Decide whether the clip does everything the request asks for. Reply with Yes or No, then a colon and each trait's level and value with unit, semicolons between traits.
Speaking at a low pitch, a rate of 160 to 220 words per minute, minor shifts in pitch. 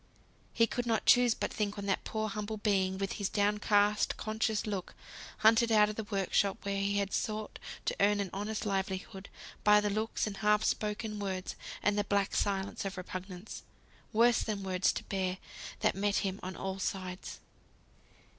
No: high, 205 Hz; average, 180 wpm; narrow, 1.7 semitones